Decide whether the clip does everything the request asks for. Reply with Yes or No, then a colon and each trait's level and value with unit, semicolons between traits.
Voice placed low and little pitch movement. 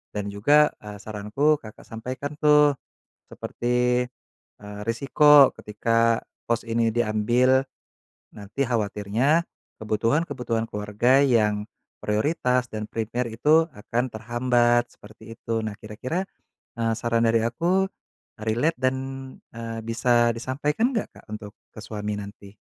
No: low, 115 Hz; average, 3.3 semitones